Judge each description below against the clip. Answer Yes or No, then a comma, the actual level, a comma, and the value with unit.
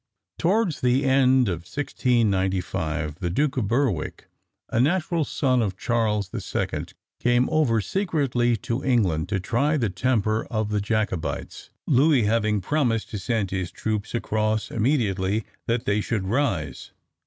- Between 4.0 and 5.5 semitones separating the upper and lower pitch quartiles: Yes, average, 4.8 semitones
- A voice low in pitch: Yes, low, 115 Hz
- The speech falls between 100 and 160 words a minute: Yes, average, 145 wpm